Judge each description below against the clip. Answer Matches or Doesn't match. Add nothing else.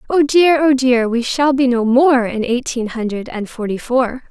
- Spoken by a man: Doesn't match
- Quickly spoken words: Matches